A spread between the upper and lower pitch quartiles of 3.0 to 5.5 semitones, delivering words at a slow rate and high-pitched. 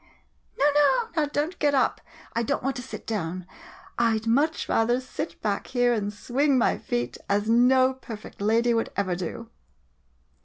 No: average, 3.8 semitones; average, 185 wpm; high, 235 Hz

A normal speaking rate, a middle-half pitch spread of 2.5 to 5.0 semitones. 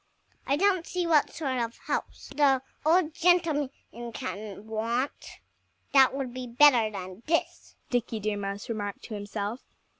No: average, 145 wpm; wide, 5.6 semitones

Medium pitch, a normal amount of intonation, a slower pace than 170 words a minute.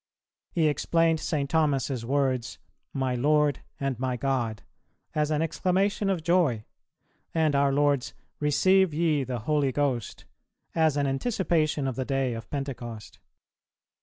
Yes: medium, 145 Hz; average, 3.3 semitones; slow, 135 wpm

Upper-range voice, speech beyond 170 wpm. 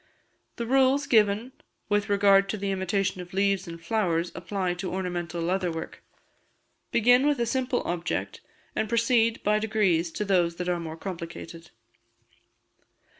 No: high, 195 Hz; average, 145 wpm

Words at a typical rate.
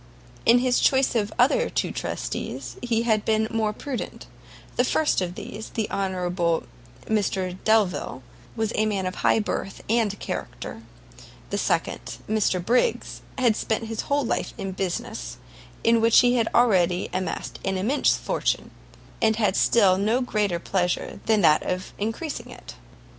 Yes: average, 155 wpm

